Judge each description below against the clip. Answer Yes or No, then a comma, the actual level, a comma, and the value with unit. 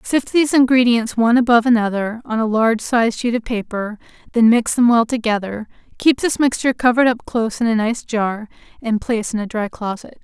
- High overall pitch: Yes, high, 230 Hz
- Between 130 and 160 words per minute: No, average, 200 wpm